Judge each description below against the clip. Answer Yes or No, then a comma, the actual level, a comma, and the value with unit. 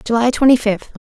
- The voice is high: Yes, high, 235 Hz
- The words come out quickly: No, average, 175 wpm